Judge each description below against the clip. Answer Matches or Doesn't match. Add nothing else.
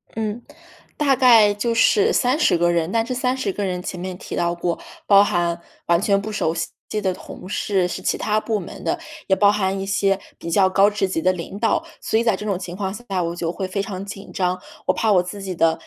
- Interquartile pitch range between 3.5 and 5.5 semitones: Doesn't match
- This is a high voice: Matches